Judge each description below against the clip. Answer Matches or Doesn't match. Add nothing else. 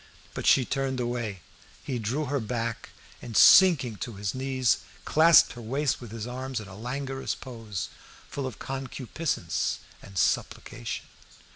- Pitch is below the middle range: Matches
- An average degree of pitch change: Matches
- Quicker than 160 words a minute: Doesn't match